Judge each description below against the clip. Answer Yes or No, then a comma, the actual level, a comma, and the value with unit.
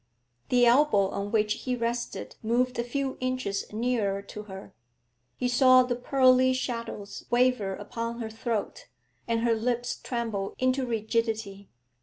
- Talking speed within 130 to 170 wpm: Yes, average, 140 wpm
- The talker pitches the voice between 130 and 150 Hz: No, high, 235 Hz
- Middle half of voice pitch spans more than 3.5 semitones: No, average, 2.9 semitones